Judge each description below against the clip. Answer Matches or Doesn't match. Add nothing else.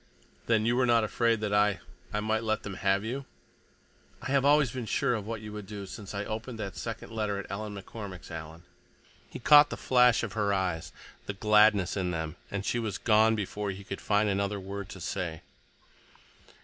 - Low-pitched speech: Matches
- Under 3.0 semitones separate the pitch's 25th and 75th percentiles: Matches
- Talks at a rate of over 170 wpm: Matches